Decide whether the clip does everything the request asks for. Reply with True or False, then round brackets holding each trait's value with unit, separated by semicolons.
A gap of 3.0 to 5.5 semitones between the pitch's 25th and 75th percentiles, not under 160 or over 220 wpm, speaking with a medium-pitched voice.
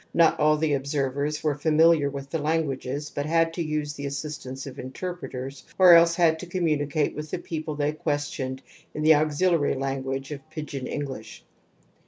False (2.5 semitones; 175 wpm; 150 Hz)